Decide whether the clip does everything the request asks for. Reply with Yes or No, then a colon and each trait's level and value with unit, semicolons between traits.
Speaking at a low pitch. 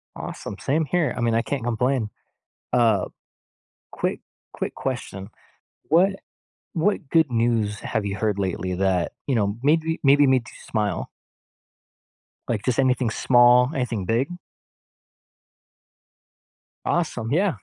Yes: low, 120 Hz